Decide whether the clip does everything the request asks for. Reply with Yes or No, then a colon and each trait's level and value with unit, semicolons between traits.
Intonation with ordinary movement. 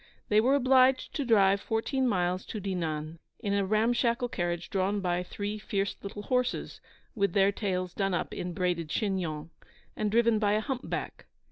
Yes: average, 4.2 semitones